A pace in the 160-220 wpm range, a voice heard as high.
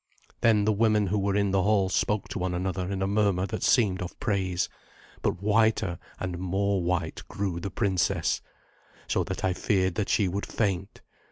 No: average, 185 wpm; very low, 95 Hz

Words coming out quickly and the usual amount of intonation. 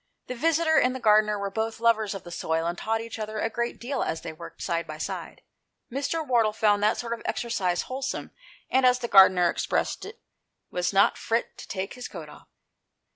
Yes: fast, 215 wpm; average, 4.3 semitones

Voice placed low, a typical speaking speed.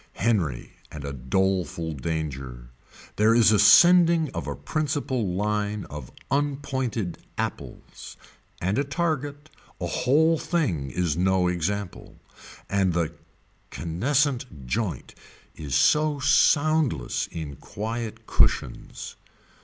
No: low, 105 Hz; slow, 105 wpm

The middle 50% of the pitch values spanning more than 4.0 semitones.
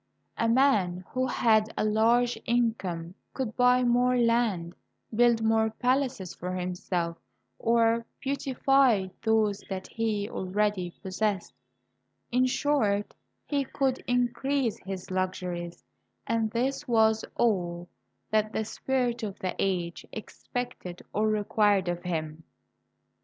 Yes: average, 4.6 semitones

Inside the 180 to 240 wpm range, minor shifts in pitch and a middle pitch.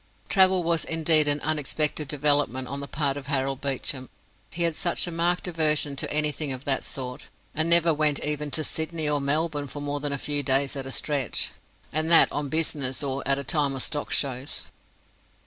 Yes: average, 200 wpm; narrow, 2.3 semitones; medium, 145 Hz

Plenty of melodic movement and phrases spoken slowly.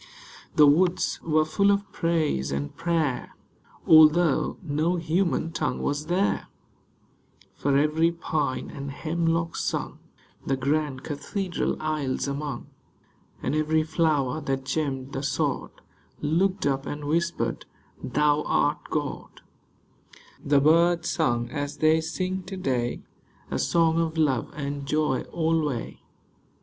No: average, 2.9 semitones; slow, 125 wpm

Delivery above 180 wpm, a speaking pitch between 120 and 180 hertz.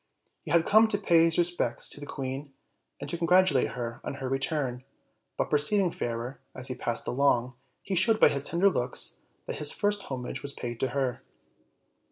Yes: average, 190 wpm; medium, 140 Hz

